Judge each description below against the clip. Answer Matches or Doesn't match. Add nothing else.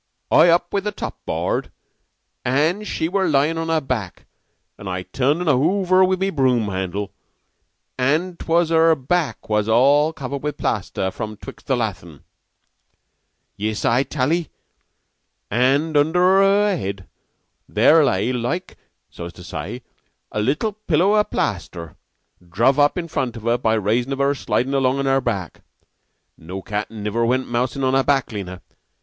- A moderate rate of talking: Matches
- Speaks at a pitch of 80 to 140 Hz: Matches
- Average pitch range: Doesn't match